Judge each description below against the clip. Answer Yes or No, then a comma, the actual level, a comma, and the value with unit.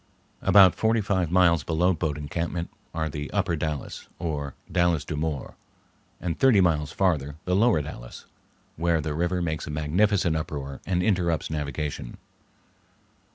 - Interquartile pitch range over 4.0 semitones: No, average, 3.3 semitones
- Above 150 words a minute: No, average, 145 wpm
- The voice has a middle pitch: No, very low, 80 Hz